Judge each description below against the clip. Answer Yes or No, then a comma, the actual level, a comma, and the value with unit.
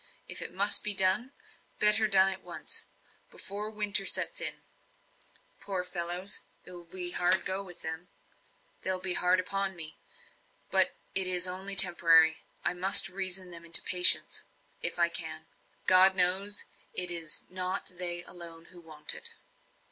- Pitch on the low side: No, medium, 185 Hz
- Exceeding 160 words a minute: No, average, 150 wpm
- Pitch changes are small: Yes, narrow, 1.7 semitones